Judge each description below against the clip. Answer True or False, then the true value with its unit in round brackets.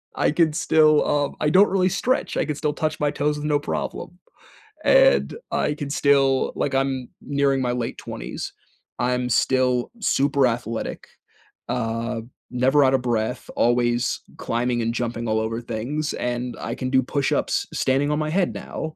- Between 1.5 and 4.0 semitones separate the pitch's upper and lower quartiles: True (3.5 semitones)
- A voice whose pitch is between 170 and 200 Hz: False (135 Hz)